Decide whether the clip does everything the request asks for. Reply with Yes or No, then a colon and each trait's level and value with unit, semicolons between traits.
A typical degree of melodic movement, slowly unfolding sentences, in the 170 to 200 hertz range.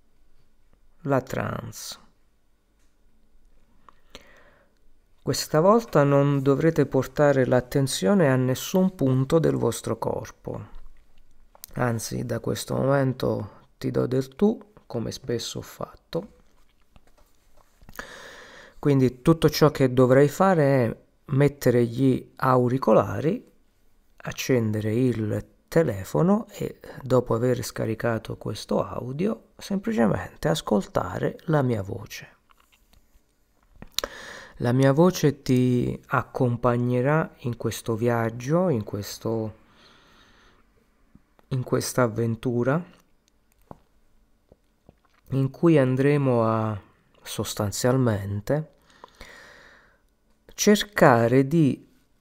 No: average, 4.0 semitones; slow, 80 wpm; low, 130 Hz